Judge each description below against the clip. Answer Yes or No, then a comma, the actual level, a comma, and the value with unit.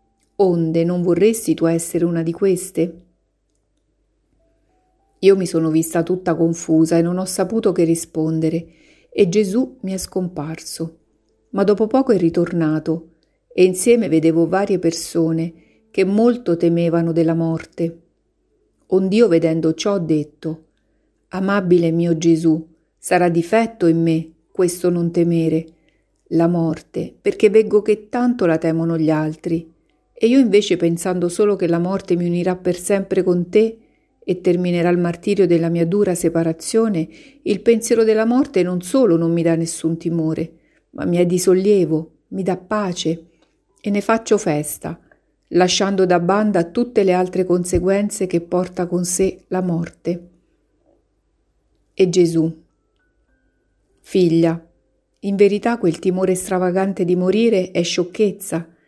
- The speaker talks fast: No, average, 135 wpm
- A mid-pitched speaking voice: Yes, medium, 175 Hz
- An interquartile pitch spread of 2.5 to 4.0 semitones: Yes, average, 2.8 semitones